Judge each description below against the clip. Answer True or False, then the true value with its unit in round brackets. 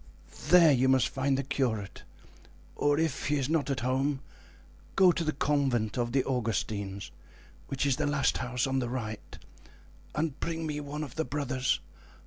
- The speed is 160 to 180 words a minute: True (170 wpm)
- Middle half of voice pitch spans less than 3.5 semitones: True (2.9 semitones)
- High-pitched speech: False (135 Hz)